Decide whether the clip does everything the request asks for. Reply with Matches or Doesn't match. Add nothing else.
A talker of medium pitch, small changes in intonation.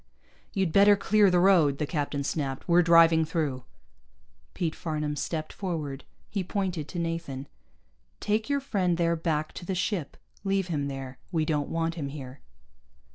Doesn't match